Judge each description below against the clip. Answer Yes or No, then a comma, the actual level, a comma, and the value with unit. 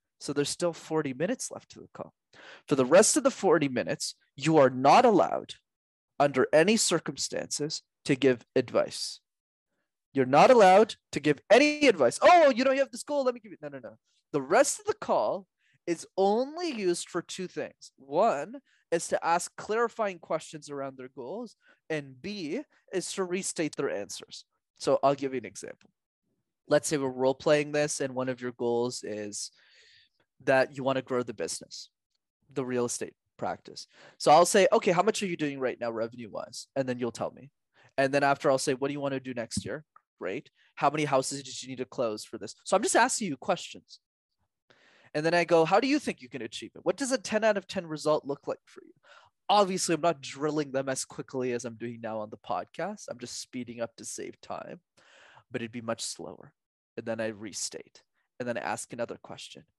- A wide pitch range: Yes, wide, 6.5 semitones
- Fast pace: Yes, fast, 215 wpm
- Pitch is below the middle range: No, medium, 150 Hz